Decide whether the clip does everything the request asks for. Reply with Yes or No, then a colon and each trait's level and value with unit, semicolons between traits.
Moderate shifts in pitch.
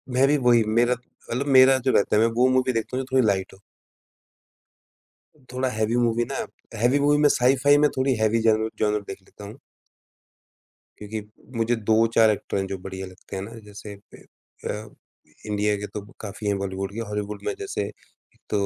Yes: average, 3.6 semitones